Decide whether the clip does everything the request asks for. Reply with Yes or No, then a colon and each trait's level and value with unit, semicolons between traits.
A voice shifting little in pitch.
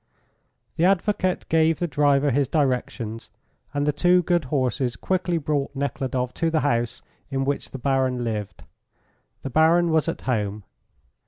No: average, 4.3 semitones